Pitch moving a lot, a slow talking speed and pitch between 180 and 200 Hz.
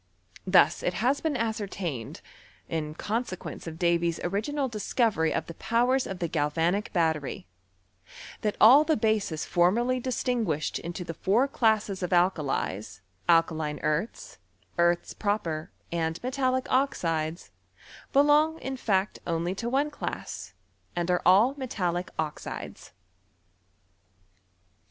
Yes: wide, 6.4 semitones; slow, 120 wpm; medium, 185 Hz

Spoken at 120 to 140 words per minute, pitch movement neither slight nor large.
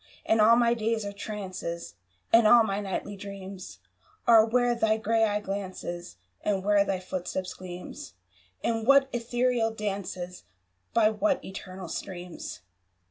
Yes: slow, 135 wpm; average, 3.3 semitones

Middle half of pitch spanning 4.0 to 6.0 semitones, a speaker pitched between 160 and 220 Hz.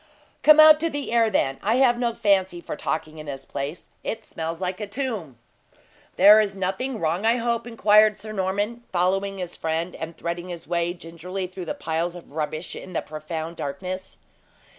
Yes: average, 4.6 semitones; medium, 185 Hz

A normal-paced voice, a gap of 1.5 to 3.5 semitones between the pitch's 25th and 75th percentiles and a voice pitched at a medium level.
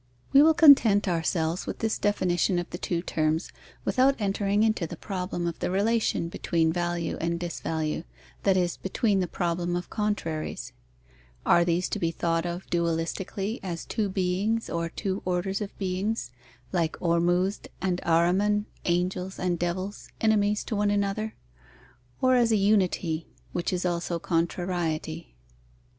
Yes: average, 150 wpm; average, 3.2 semitones; medium, 180 Hz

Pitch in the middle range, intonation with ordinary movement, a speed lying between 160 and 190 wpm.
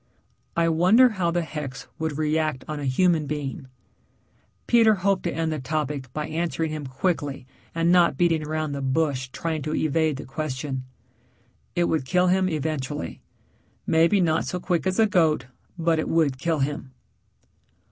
Yes: medium, 155 Hz; average, 3.0 semitones; average, 165 wpm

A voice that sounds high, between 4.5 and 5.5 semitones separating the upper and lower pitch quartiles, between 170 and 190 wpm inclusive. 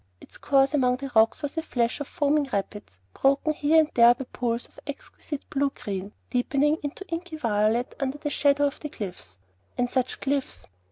No: very high, 275 Hz; average, 3.7 semitones; average, 185 wpm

